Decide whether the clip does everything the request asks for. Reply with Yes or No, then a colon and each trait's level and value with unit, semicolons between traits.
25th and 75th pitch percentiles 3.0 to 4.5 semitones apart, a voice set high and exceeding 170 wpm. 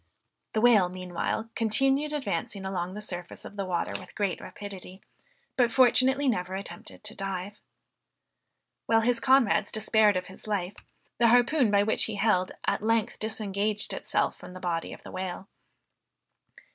No: average, 3.5 semitones; high, 210 Hz; average, 155 wpm